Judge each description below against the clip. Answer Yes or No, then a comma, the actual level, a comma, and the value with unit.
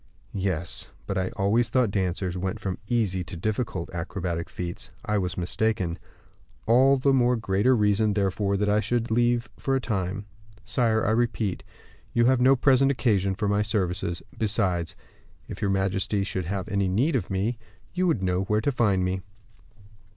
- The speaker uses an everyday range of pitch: Yes, average, 4.0 semitones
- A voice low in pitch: Yes, low, 100 Hz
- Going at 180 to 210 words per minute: No, average, 170 wpm